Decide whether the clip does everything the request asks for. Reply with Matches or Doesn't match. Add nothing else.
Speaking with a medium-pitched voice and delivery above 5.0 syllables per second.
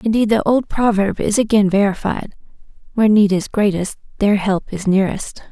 Doesn't match